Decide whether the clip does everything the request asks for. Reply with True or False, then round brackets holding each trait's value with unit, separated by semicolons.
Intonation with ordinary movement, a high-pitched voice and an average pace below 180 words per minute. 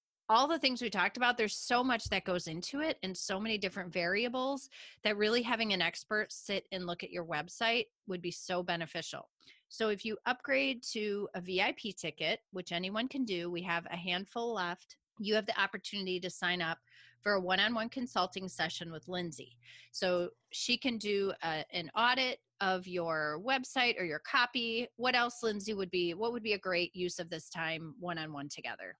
False (4.9 semitones; 195 Hz; 190 wpm)